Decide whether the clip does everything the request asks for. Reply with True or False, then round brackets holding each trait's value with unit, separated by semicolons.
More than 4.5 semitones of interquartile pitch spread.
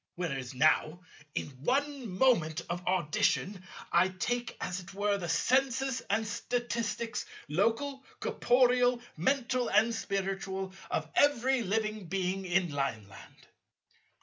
True (5.5 semitones)